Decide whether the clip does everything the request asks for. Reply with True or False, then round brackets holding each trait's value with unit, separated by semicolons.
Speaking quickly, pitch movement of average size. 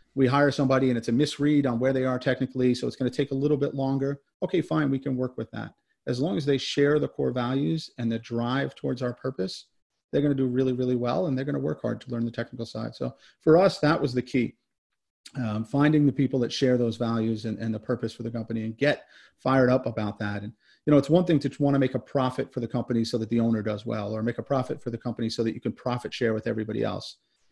True (275 wpm; 3.2 semitones)